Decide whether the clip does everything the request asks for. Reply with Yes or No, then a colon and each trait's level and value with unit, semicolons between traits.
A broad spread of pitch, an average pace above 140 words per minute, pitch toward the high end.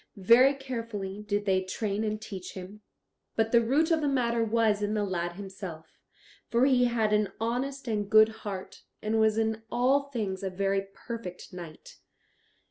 No: average, 3.1 semitones; average, 170 wpm; high, 215 Hz